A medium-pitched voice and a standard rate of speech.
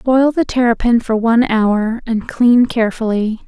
No: high, 235 Hz; average, 155 wpm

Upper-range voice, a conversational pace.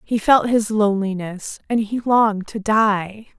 Yes: high, 210 Hz; average, 160 wpm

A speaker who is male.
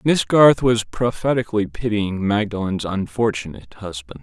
Yes: male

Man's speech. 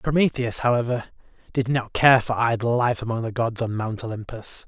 Yes: male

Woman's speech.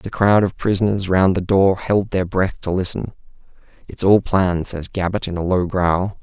No: male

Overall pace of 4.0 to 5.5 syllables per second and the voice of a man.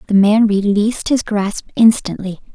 No: 4.7 syllables/s; female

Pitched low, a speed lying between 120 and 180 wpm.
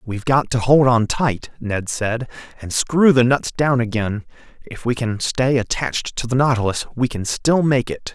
No: low, 120 Hz; average, 200 wpm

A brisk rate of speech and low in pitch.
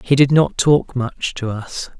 Yes: fast, 210 wpm; low, 130 Hz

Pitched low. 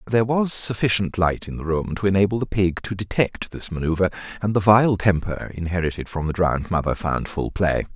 Yes: very low, 95 Hz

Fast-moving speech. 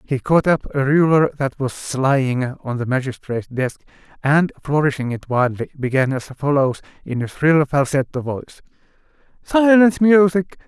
No: average, 145 wpm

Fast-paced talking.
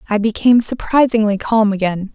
No: average, 140 wpm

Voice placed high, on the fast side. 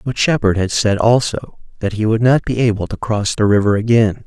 No: low, 110 Hz; fast, 225 wpm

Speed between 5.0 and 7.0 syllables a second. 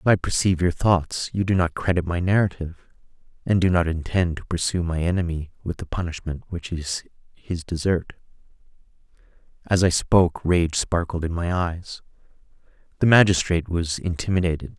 Yes: 5.4 syllables/s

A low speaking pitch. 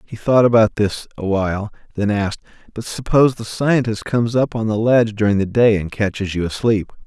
Yes: low, 110 Hz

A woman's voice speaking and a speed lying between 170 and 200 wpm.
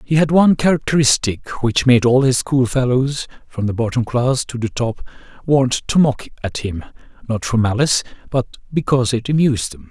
No: male; average, 175 wpm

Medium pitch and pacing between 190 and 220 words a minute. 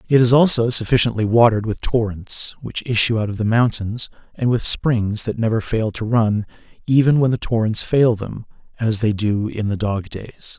No: low, 115 Hz; average, 195 wpm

